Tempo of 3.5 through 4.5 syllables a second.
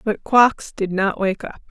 Yes: 4.1 syllables/s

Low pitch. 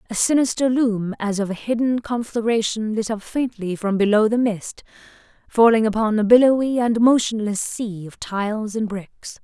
No: high, 220 Hz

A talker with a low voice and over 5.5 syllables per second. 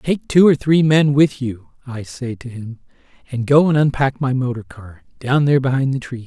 No: low, 130 Hz; 5.0 syllables/s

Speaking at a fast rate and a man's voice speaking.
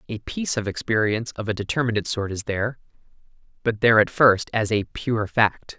No: average, 185 wpm; male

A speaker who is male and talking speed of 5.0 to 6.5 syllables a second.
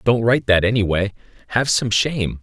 Yes: male; 5.8 syllables/s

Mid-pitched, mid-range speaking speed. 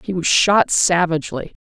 Yes: medium, 175 Hz; average, 150 wpm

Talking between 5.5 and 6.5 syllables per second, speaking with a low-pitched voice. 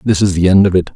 No: 7.1 syllables/s; very low, 95 Hz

